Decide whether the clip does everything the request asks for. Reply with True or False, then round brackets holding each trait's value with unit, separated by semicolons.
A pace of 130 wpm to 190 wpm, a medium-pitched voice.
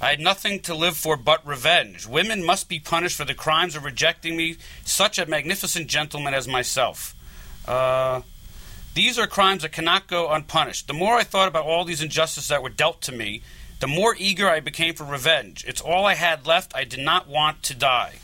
False (205 wpm; 155 Hz)